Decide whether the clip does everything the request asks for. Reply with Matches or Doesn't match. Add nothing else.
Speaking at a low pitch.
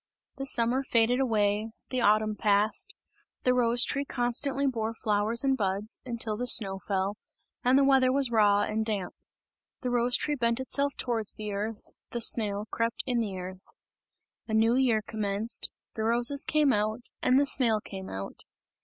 Doesn't match